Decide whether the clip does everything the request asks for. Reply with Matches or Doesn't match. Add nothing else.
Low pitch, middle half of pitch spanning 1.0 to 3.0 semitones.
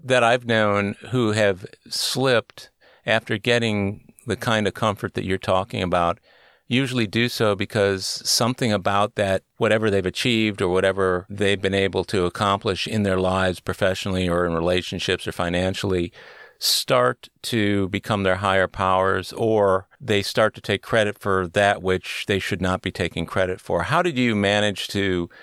Matches